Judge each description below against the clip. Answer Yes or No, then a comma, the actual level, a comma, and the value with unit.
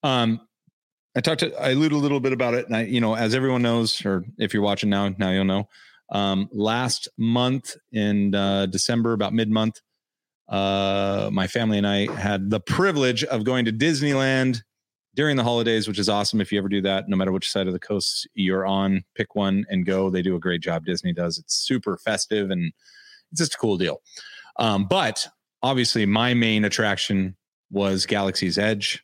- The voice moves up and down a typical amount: Yes, average, 3.8 semitones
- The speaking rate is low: No, average, 200 wpm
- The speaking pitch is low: Yes, low, 105 Hz